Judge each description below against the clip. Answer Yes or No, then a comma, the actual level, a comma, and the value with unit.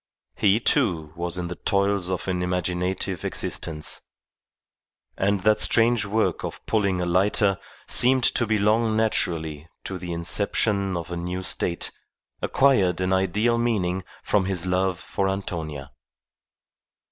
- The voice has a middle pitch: No, very low, 95 Hz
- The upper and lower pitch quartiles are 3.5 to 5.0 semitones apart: No, average, 2.9 semitones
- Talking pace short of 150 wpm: Yes, slow, 135 wpm